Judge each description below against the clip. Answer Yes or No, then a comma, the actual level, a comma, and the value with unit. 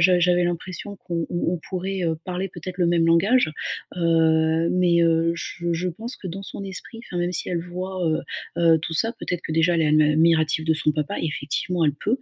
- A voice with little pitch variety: Yes, narrow, 2.0 semitones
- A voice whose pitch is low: No, medium, 170 Hz